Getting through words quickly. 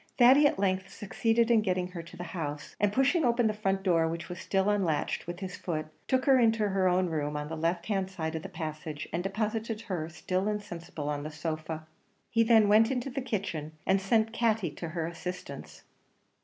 Yes: fast, 210 wpm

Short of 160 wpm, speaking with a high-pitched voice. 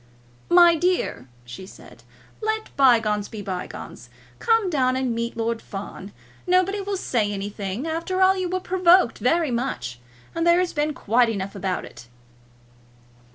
Yes: average, 150 wpm; very high, 260 Hz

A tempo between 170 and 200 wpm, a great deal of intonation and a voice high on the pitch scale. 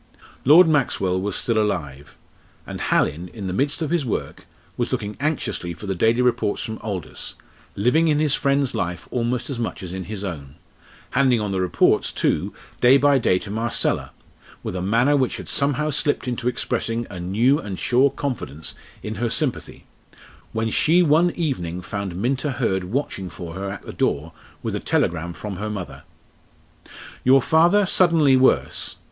No: average, 175 wpm; wide, 6.6 semitones; low, 115 Hz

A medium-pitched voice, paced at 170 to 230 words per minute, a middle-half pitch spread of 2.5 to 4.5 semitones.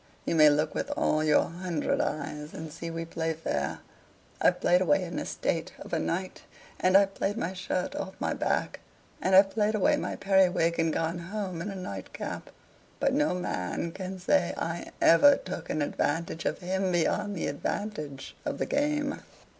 Yes: medium, 180 Hz; average, 180 wpm; average, 3.0 semitones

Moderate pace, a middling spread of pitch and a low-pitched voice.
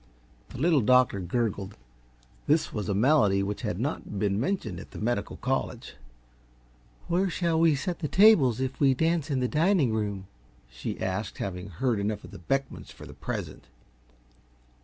No: average, 165 wpm; wide, 7.1 semitones; low, 125 Hz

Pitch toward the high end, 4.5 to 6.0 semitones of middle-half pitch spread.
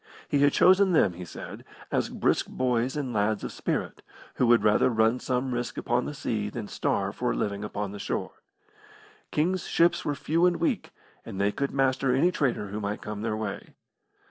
No: low, 120 Hz; average, 5.2 semitones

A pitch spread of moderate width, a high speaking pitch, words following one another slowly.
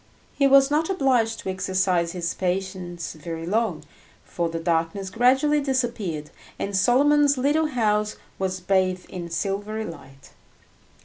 No: wide, 6.4 semitones; high, 195 Hz; slow, 130 wpm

